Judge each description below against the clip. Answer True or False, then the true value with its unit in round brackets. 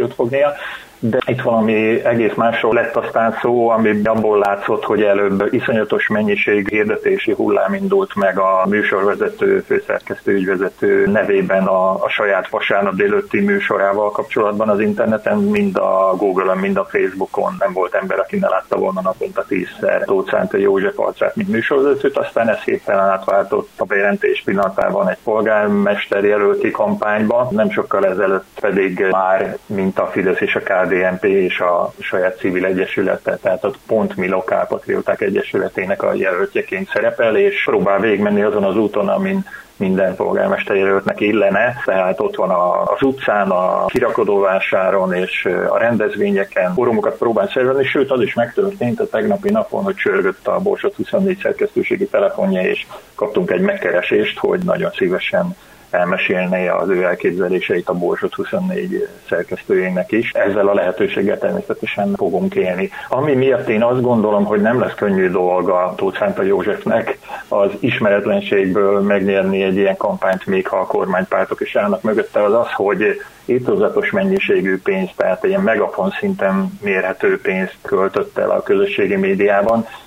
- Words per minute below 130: False (150 wpm)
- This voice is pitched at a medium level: True (145 Hz)